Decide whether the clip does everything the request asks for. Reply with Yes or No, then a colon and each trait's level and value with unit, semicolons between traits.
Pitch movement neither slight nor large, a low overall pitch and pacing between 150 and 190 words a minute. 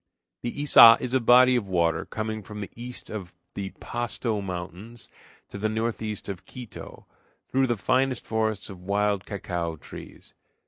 Yes: average, 3.6 semitones; low, 110 Hz; average, 155 wpm